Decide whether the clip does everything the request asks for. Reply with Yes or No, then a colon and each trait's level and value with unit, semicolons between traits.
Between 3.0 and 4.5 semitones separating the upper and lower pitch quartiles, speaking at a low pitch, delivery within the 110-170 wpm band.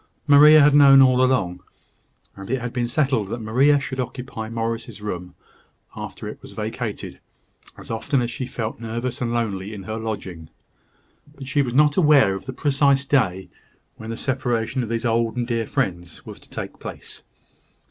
No: average, 3.5 semitones; low, 120 Hz; average, 180 wpm